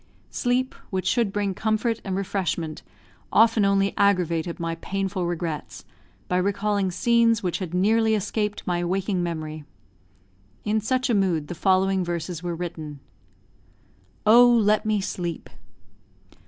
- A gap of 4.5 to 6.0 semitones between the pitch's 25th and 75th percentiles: No, average, 3.5 semitones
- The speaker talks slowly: Yes, slow, 130 wpm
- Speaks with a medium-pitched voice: No, high, 195 Hz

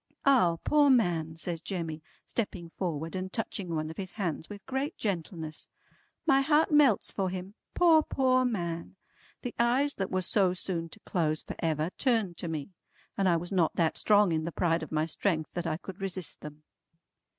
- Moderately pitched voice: Yes, medium, 180 Hz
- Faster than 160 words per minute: Yes, average, 185 wpm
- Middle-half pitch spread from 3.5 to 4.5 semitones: No, average, 5.2 semitones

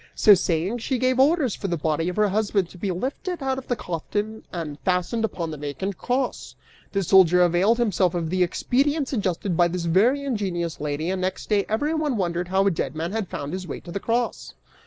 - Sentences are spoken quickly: Yes, fast, 215 wpm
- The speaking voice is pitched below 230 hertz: Yes, high, 190 Hz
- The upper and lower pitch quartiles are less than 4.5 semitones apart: No, average, 5.3 semitones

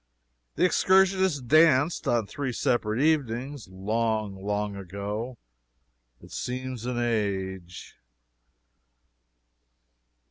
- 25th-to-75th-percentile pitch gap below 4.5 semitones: No, average, 5.3 semitones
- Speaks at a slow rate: Yes, slow, 80 wpm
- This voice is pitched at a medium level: No, low, 120 Hz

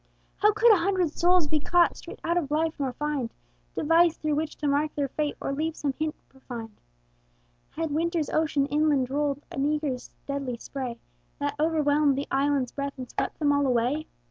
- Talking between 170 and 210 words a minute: Yes, average, 185 wpm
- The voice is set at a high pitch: Yes, very high, 295 Hz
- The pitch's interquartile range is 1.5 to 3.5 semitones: Yes, narrow, 2.4 semitones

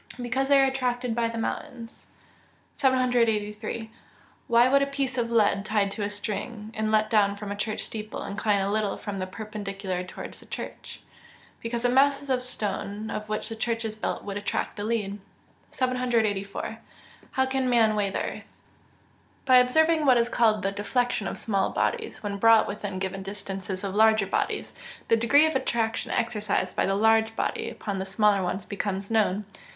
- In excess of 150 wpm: Yes, average, 180 wpm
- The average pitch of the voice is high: Yes, high, 220 Hz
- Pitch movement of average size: Yes, average, 3.2 semitones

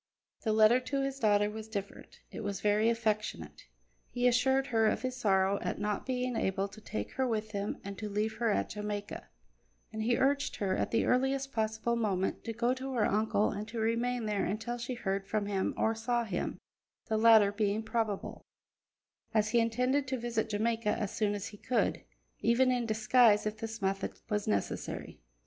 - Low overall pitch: No, high, 220 Hz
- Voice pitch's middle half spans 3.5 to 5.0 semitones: No, narrow, 2.6 semitones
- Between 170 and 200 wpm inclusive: Yes, average, 190 wpm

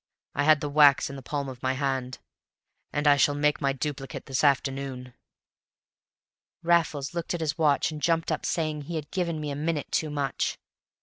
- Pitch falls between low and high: Yes, medium, 145 Hz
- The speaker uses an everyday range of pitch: No, narrow, 2.2 semitones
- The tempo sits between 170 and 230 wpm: Yes, average, 190 wpm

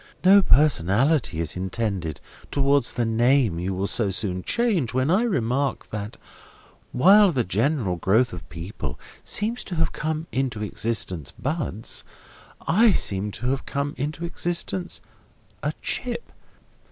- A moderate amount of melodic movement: No, wide, 8.0 semitones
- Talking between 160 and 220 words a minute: No, slow, 135 wpm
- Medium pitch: No, low, 125 Hz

